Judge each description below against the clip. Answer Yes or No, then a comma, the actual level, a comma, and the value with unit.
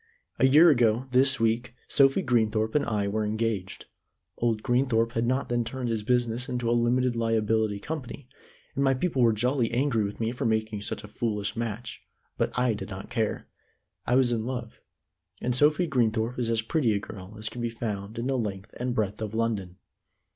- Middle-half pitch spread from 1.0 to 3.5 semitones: Yes, narrow, 2.5 semitones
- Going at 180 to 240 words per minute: Yes, average, 195 wpm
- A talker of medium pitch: No, low, 115 Hz